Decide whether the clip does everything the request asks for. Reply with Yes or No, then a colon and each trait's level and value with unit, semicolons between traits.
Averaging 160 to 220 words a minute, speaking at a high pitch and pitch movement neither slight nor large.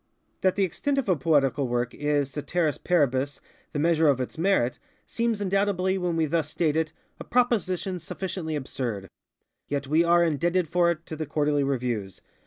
No: average, 170 wpm; medium, 160 Hz; average, 4.3 semitones